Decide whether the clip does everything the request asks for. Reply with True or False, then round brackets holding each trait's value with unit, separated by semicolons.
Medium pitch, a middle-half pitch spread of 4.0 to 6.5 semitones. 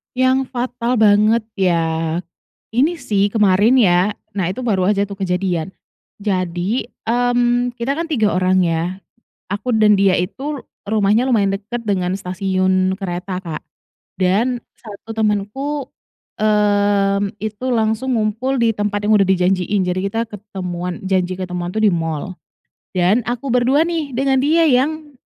False (205 Hz; 4.5 semitones)